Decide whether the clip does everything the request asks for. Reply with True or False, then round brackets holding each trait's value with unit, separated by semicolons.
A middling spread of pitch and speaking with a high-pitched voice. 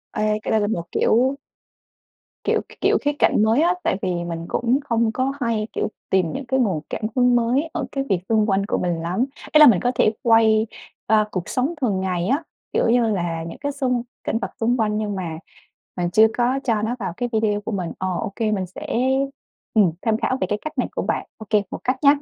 True (4.4 semitones; 220 Hz)